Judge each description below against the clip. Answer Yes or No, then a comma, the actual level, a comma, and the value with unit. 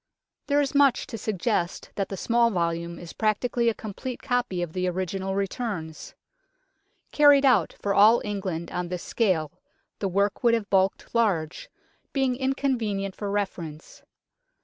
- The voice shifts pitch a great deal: No, average, 4.7 semitones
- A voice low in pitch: No, high, 200 Hz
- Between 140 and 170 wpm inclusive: Yes, average, 150 wpm